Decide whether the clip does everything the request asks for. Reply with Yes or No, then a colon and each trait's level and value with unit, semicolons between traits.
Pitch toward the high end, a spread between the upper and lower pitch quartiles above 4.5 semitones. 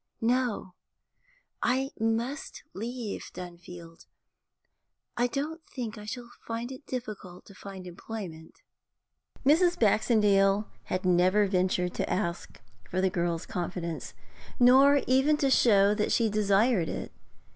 Yes: high, 210 Hz; average, 5.2 semitones